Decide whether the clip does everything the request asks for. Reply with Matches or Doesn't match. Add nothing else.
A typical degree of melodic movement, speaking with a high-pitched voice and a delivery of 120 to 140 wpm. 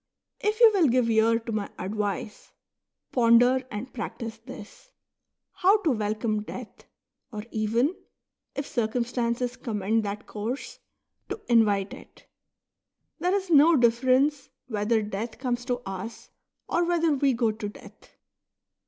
Matches